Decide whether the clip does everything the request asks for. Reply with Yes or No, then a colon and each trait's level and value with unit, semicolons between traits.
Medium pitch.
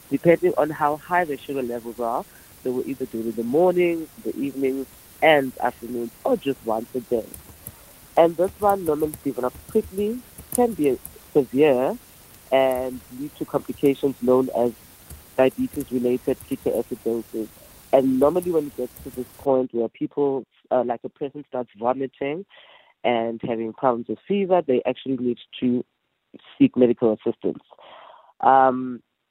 No: low, 130 Hz